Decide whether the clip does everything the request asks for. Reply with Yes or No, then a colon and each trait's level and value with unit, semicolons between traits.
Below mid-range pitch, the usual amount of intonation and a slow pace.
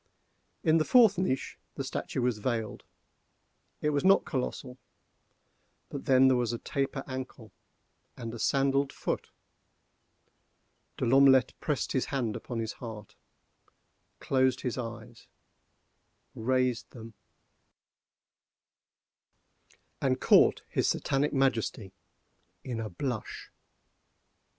Yes: low, 130 Hz; average, 3.0 semitones; slow, 100 wpm